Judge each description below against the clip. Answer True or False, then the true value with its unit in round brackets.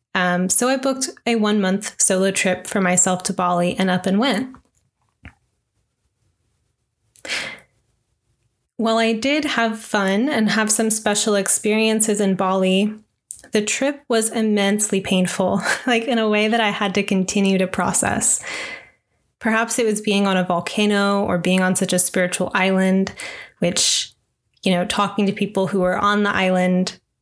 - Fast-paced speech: False (155 wpm)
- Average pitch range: True (3.1 semitones)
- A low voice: False (200 Hz)